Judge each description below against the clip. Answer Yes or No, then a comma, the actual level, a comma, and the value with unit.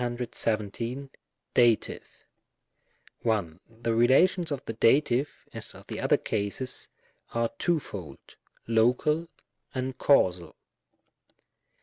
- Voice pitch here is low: Yes, low, 115 Hz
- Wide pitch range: No, average, 3.8 semitones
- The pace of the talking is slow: Yes, slow, 90 wpm